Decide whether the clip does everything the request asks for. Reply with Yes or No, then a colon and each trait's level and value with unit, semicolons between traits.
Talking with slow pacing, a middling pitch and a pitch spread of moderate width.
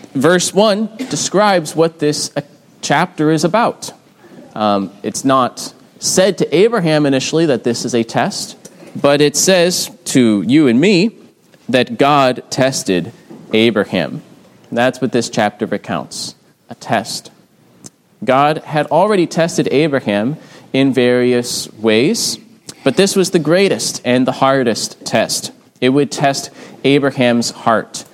No: slow, 130 wpm; medium, 150 Hz; wide, 6.2 semitones